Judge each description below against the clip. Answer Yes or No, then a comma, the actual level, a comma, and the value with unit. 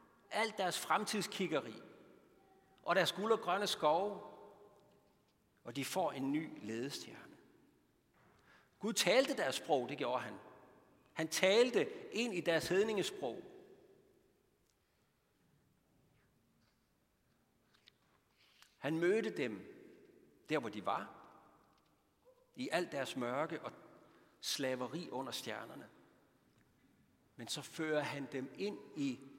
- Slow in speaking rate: Yes, slow, 100 wpm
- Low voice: No, high, 190 Hz